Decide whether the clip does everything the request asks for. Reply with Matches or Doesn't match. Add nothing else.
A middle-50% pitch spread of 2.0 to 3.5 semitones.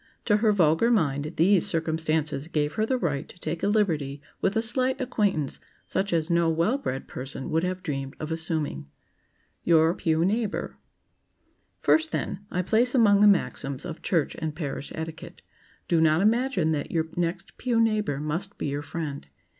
Doesn't match